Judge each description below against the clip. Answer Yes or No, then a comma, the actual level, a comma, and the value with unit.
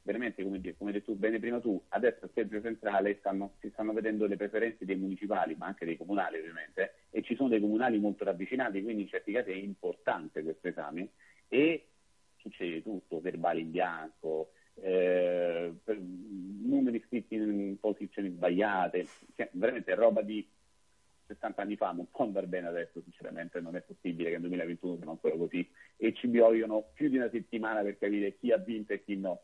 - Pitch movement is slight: No, average, 3.4 semitones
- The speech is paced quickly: Yes, fast, 180 wpm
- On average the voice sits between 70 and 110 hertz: Yes, low, 100 Hz